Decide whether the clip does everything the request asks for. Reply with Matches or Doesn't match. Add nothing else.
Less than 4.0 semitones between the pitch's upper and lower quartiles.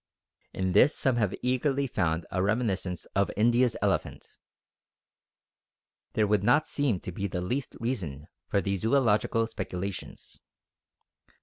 Doesn't match